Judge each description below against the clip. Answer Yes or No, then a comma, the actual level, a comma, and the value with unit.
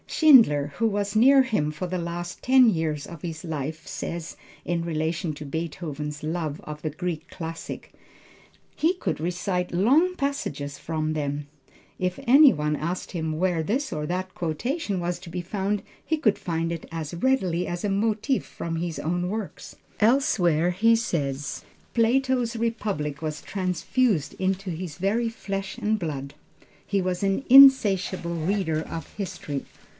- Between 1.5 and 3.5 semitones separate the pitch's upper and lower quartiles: No, average, 5.3 semitones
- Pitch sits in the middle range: Yes, medium, 180 Hz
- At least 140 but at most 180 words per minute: Yes, average, 155 wpm